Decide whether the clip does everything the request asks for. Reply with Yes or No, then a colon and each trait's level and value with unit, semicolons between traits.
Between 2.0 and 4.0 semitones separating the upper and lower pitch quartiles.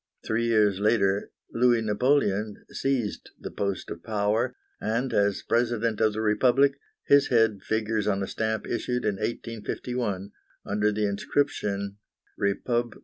Yes: average, 2.7 semitones